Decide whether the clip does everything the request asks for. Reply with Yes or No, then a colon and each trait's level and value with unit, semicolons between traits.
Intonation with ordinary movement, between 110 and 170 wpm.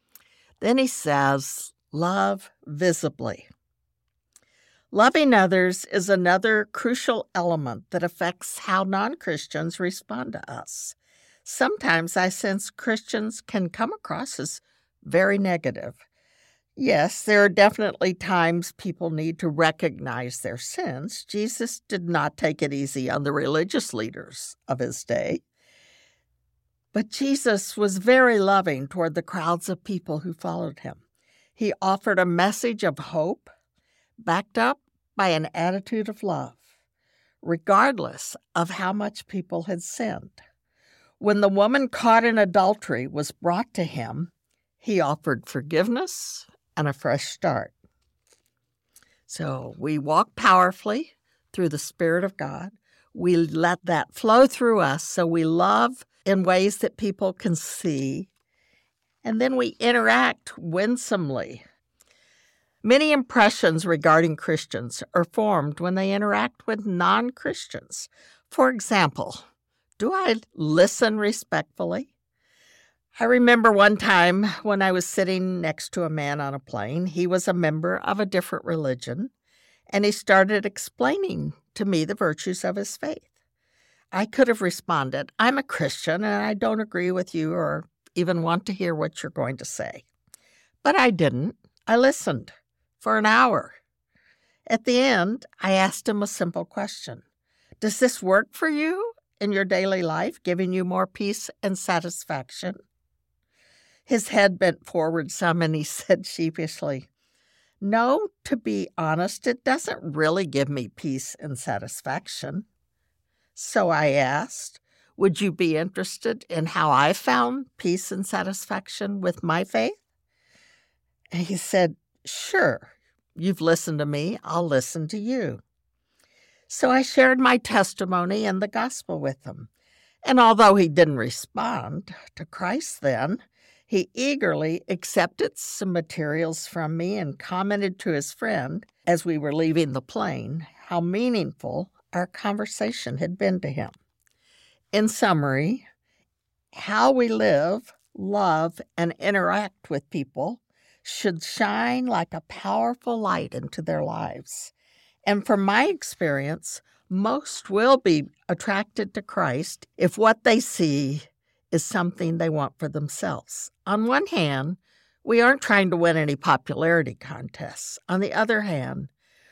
Yes: average, 4.7 semitones; slow, 135 wpm